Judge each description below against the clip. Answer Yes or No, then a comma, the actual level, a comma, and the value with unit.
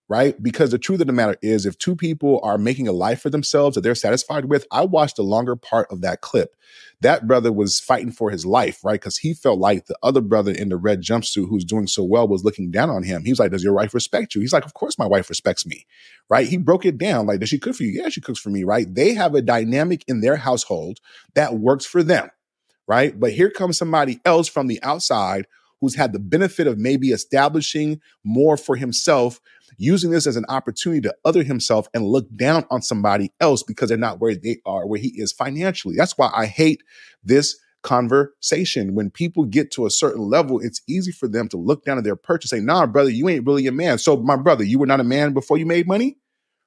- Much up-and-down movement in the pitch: Yes, wide, 6.0 semitones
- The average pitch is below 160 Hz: Yes, low, 135 Hz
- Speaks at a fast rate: Yes, fast, 240 wpm